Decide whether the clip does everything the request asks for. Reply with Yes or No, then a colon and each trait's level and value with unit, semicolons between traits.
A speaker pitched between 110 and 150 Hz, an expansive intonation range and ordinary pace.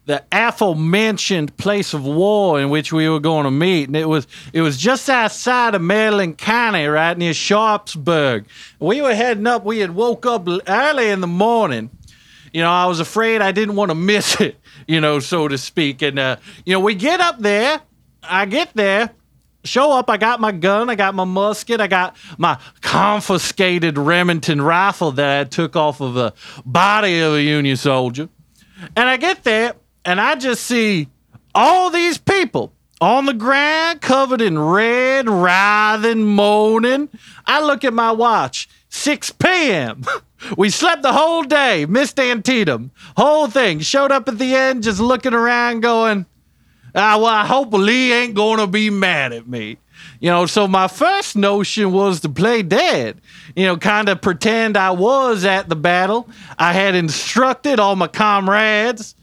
No: high, 205 Hz; wide, 5.9 semitones; average, 175 wpm